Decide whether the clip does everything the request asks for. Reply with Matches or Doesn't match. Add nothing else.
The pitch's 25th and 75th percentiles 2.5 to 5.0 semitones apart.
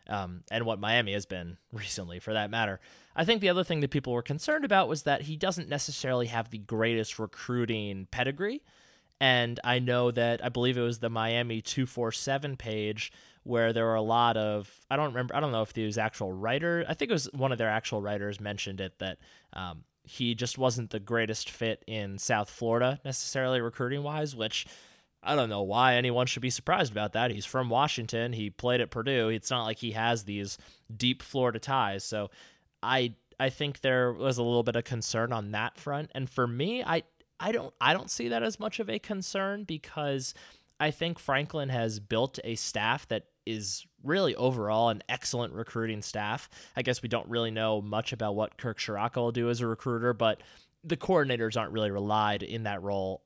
Matches